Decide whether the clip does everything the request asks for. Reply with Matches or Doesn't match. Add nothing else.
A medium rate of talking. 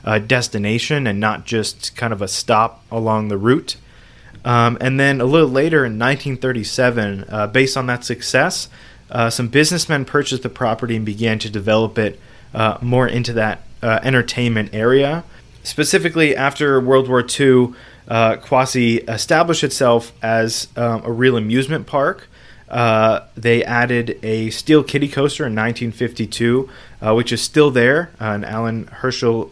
Matches